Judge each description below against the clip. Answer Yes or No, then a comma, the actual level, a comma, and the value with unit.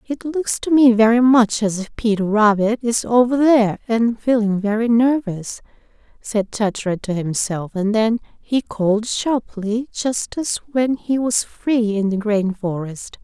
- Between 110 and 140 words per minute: No, average, 165 wpm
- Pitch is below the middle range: No, high, 225 Hz